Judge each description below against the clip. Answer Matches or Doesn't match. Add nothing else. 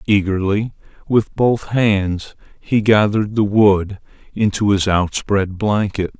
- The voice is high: Doesn't match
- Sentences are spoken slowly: Matches